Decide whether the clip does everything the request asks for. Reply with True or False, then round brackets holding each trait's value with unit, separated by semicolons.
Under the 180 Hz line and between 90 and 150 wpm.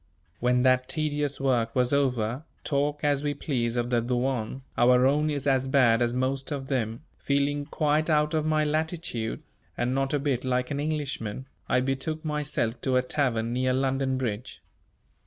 False (135 Hz; 175 wpm)